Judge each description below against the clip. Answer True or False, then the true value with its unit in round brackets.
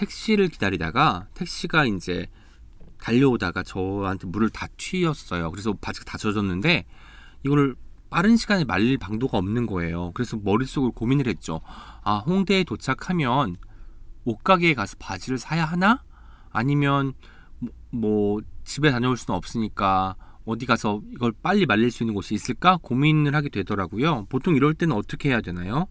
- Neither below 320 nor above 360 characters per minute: True (340 characters per minute)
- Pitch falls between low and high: False (115 Hz)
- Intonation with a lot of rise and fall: True (6.5 semitones)